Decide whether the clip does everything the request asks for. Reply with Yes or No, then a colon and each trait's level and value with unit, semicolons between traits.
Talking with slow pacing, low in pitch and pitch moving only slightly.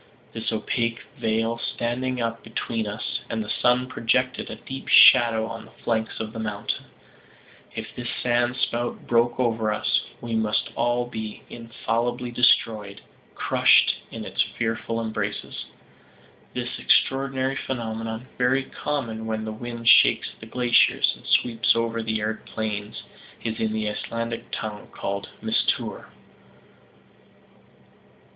Yes: slow, 130 wpm; low, 115 Hz; narrow, 1.6 semitones